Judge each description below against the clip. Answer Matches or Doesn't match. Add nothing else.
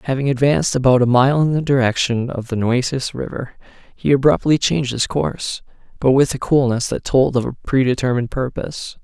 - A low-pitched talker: Matches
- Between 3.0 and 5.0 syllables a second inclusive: Doesn't match